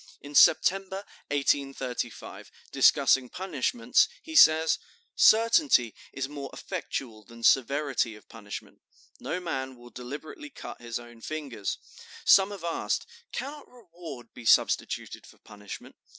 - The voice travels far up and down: Yes, wide, 7.7 semitones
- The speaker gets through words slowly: Yes, slow, 120 wpm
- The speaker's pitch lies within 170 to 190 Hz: No, medium, 140 Hz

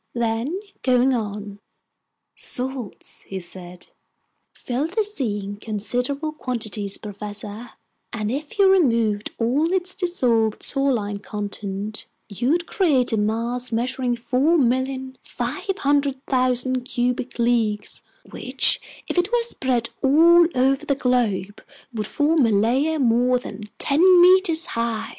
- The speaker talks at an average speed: No, slow, 115 wpm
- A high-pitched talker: Yes, very high, 250 Hz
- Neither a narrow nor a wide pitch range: Yes, average, 4.6 semitones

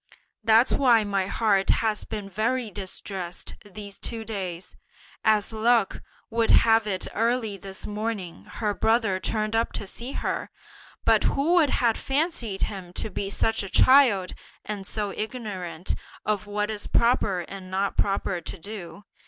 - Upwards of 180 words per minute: No, average, 155 wpm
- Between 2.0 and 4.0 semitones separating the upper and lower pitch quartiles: Yes, average, 2.7 semitones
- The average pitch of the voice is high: Yes, high, 210 Hz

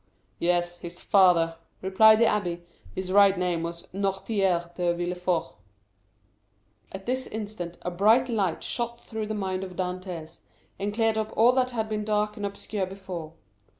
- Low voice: No, high, 190 Hz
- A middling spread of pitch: Yes, average, 3.5 semitones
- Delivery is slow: No, average, 155 wpm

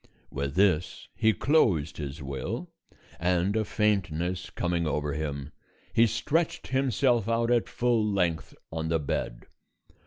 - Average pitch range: No, wide, 6.5 semitones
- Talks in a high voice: No, very low, 90 Hz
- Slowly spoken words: Yes, slow, 130 wpm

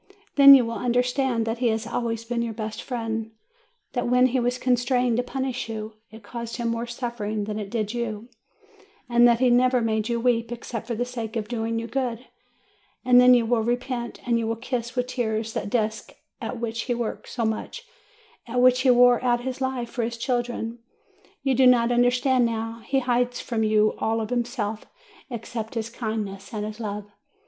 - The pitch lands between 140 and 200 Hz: No, high, 235 Hz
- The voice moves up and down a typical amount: No, narrow, 1.7 semitones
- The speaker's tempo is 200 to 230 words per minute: Yes, fast, 205 wpm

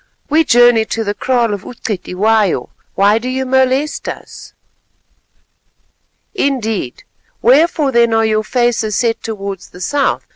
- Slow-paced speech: Yes, slow, 125 wpm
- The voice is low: No, high, 230 Hz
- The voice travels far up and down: No, average, 3.4 semitones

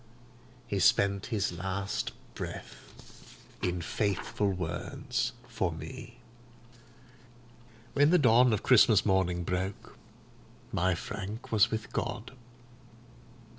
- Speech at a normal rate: No, slow, 95 wpm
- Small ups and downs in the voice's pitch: No, average, 3.6 semitones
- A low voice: Yes, low, 100 Hz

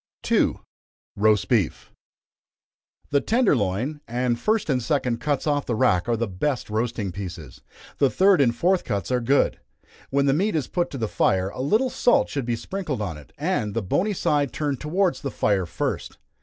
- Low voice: Yes, low, 130 Hz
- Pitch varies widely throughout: Yes, wide, 5.8 semitones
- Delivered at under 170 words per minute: No, average, 185 wpm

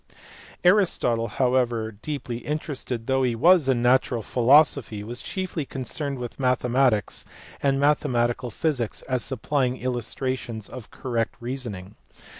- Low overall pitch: Yes, low, 125 Hz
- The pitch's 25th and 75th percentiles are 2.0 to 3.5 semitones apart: Yes, average, 2.7 semitones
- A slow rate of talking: Yes, slow, 120 wpm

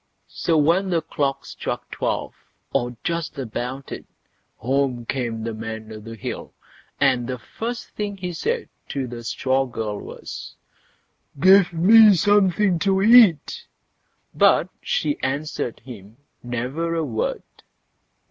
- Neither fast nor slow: No, slow, 130 wpm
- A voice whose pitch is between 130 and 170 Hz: Yes, medium, 140 Hz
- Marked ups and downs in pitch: Yes, wide, 7.6 semitones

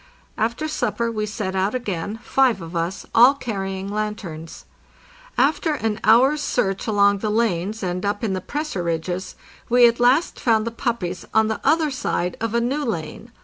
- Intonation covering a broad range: No, average, 4.1 semitones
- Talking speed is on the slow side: No, average, 175 wpm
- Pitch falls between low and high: No, high, 215 Hz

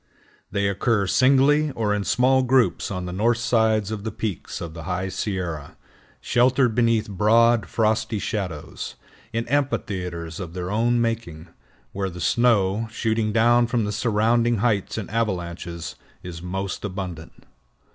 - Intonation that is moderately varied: Yes, average, 4.0 semitones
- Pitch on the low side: Yes, low, 105 Hz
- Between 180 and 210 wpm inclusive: No, average, 145 wpm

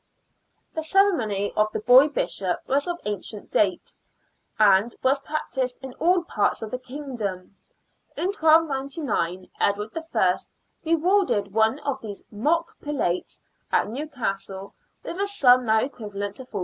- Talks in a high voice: Yes, very high, 250 Hz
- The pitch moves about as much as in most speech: No, wide, 6.7 semitones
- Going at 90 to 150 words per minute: Yes, average, 140 wpm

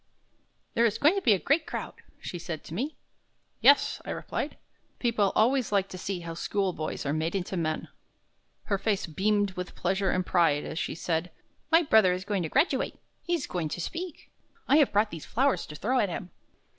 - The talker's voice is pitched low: No, high, 195 Hz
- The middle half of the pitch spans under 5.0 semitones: No, wide, 5.6 semitones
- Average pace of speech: Yes, average, 195 wpm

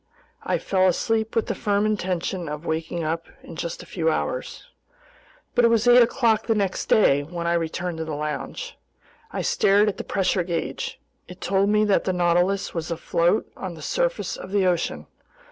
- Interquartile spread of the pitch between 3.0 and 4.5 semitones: Yes, average, 4.0 semitones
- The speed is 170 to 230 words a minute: Yes, average, 190 wpm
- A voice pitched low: No, medium, 185 Hz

